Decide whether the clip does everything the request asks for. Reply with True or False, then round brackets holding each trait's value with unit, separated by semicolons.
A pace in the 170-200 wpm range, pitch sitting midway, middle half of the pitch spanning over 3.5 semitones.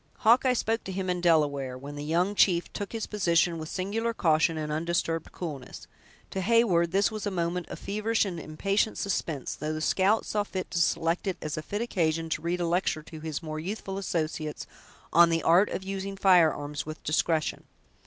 True (195 wpm; 170 Hz; 4.0 semitones)